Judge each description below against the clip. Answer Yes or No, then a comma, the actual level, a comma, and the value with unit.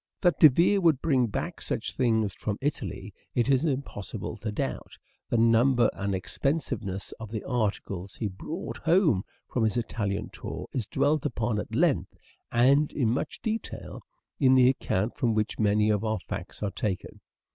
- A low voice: Yes, low, 115 Hz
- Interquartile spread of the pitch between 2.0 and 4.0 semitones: No, average, 4.7 semitones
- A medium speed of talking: Yes, average, 170 wpm